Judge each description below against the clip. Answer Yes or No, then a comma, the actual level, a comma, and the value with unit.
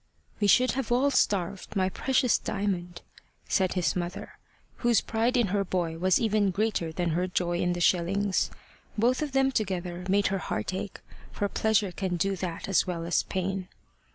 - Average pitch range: Yes, average, 3.3 semitones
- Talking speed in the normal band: Yes, average, 180 wpm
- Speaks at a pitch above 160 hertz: Yes, high, 190 Hz